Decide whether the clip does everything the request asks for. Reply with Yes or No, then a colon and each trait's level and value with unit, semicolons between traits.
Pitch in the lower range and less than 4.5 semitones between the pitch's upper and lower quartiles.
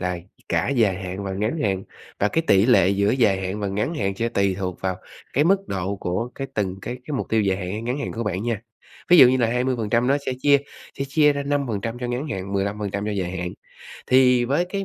No: low, 110 Hz; average, 5.0 semitones